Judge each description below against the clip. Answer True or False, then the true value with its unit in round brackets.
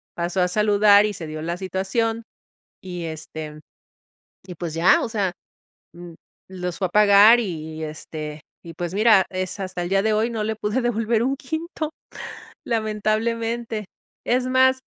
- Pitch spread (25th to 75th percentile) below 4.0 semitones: False (4.4 semitones)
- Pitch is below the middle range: False (200 Hz)